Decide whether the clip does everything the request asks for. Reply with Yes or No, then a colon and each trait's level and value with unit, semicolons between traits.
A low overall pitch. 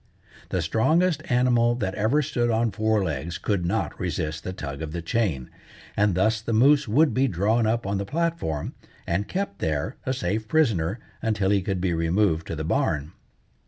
Yes: low, 105 Hz